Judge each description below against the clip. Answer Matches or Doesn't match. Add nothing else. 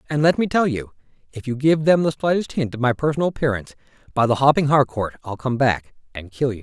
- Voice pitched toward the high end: Doesn't match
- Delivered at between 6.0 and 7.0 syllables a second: Matches